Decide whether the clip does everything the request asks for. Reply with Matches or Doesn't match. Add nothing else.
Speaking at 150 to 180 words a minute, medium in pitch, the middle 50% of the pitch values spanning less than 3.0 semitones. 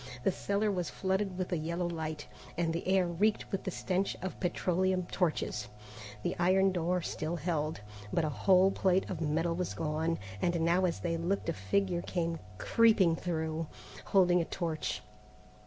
Matches